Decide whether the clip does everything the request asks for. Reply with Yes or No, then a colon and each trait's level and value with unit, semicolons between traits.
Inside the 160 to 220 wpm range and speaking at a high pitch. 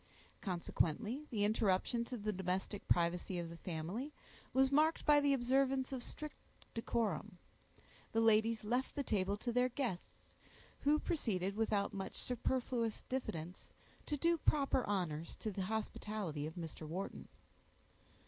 No: average, 140 wpm; high, 220 Hz